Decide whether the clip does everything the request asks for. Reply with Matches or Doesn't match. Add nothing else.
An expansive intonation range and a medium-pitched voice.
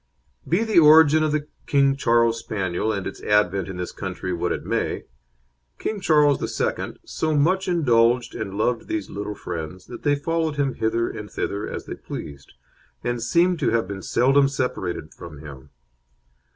Doesn't match